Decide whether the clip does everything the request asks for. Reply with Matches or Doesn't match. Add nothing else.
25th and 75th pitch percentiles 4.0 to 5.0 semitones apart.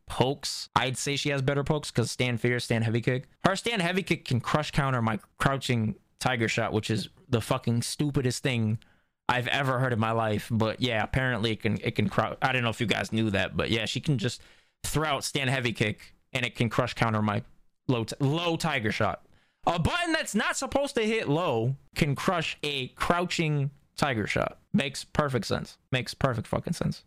Matches